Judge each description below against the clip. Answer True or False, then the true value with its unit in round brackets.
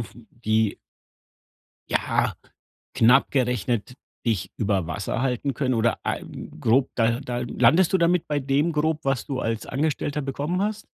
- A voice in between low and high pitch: False (130 Hz)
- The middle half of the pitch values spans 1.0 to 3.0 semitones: False (4.4 semitones)